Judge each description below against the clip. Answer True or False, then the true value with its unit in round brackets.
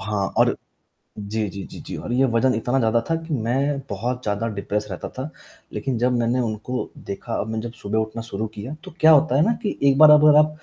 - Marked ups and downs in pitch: False (4.0 semitones)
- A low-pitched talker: True (120 Hz)